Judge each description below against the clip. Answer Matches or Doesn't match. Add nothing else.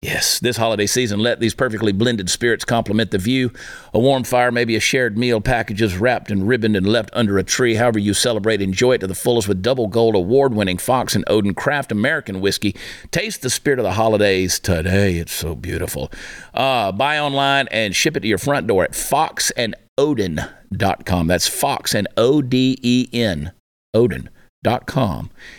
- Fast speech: Doesn't match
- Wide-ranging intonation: Doesn't match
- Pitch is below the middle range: Matches